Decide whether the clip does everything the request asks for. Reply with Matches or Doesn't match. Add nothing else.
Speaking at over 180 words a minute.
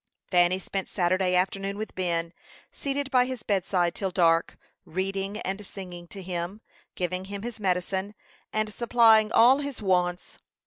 Doesn't match